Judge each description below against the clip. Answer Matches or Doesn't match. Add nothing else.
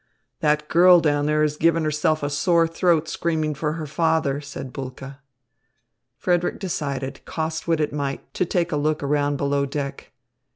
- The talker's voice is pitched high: Doesn't match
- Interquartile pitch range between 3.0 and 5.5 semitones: Doesn't match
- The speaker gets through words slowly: Doesn't match